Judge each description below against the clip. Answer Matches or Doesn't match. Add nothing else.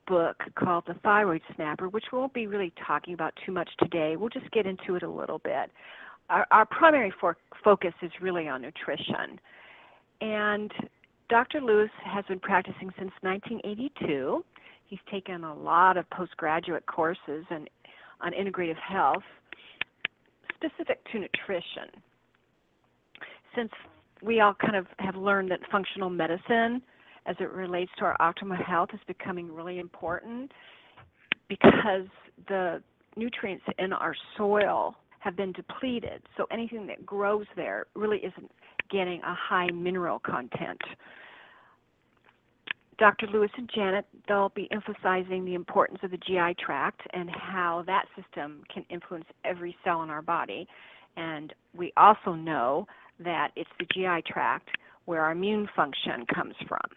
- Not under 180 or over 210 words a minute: Doesn't match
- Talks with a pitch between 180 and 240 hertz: Matches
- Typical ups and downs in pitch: Matches